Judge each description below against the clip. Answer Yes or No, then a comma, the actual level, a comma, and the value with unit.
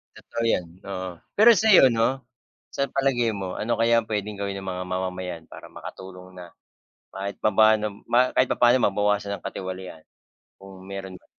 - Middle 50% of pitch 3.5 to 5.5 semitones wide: Yes, average, 3.8 semitones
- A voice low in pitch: Yes, low, 100 Hz